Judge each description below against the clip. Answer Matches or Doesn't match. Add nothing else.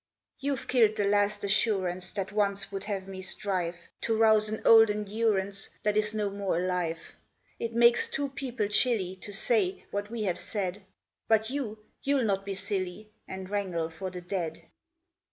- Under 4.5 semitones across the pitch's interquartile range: Matches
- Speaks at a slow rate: Doesn't match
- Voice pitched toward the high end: Matches